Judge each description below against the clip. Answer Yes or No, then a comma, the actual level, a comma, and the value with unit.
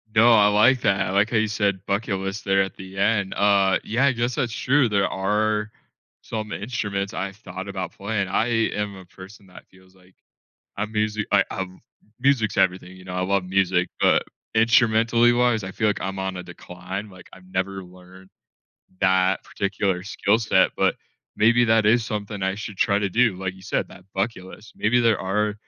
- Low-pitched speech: Yes, low, 100 Hz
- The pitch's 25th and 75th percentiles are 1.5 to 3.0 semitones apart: Yes, narrow, 2.6 semitones